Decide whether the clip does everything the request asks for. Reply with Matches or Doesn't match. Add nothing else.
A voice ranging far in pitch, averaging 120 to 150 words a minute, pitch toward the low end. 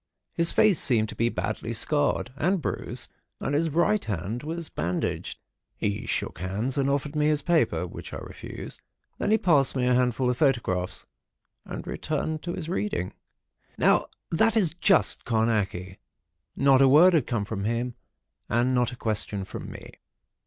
Doesn't match